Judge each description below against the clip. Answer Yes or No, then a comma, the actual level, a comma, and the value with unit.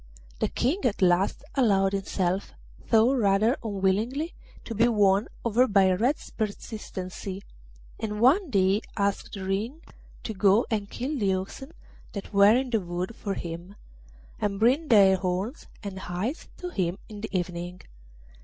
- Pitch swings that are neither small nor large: Yes, average, 3.5 semitones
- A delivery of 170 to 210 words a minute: No, average, 145 wpm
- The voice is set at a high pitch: Yes, high, 200 Hz